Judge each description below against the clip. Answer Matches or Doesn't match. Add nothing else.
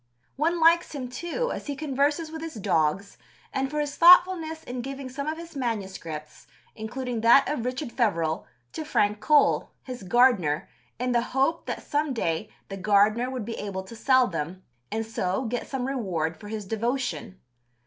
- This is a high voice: Matches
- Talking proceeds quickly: Doesn't match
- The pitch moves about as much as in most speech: Doesn't match